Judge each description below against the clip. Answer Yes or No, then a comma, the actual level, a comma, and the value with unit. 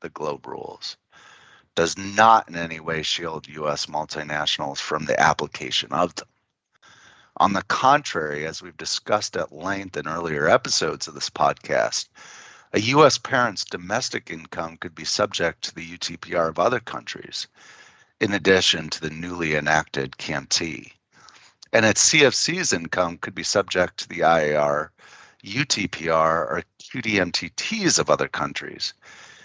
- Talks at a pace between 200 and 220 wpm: No, slow, 135 wpm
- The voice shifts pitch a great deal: No, average, 3.5 semitones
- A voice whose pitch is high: No, very low, 80 Hz